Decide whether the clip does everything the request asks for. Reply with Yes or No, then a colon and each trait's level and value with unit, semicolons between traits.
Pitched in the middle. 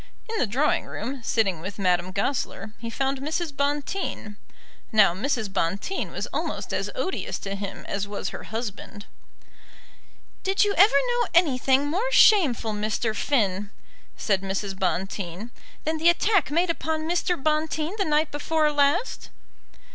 No: very high, 270 Hz